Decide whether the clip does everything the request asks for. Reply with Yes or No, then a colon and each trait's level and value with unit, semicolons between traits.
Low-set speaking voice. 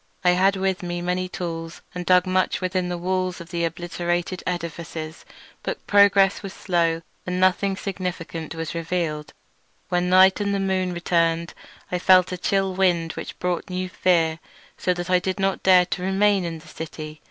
No: medium, 180 Hz